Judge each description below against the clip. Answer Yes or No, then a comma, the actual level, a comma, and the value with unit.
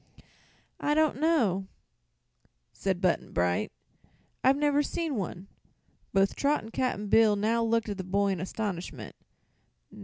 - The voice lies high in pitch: Yes, high, 210 Hz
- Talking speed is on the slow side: Yes, slow, 130 wpm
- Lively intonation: Yes, wide, 6.1 semitones